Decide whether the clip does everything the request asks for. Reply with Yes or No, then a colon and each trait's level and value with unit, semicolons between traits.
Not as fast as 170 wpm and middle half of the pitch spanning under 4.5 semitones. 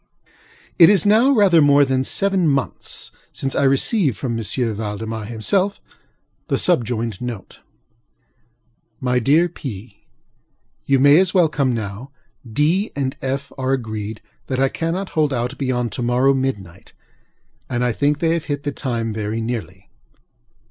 No: average, 150 wpm; average, 5.0 semitones